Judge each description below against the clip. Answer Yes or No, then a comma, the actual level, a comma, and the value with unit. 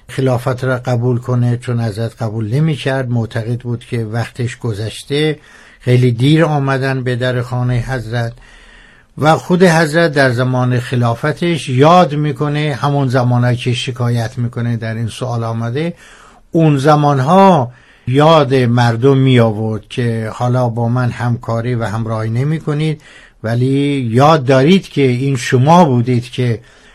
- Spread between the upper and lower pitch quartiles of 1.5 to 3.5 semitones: Yes, average, 3.2 semitones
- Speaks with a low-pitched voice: Yes, low, 125 Hz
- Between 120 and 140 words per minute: Yes, average, 135 wpm